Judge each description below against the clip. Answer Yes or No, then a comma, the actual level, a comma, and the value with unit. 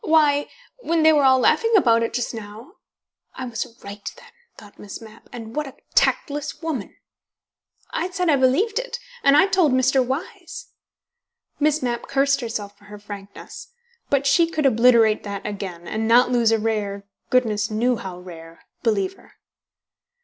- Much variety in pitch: Yes, wide, 5.9 semitones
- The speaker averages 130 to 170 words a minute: Yes, average, 165 wpm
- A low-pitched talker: No, high, 245 Hz